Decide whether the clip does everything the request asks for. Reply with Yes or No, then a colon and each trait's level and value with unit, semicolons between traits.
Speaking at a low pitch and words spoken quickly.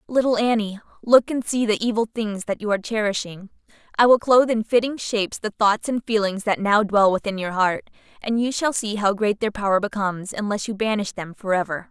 No: high, 215 Hz; fast, 215 wpm